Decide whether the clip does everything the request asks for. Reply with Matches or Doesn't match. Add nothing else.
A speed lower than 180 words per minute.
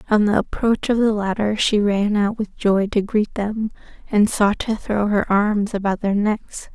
Doesn't match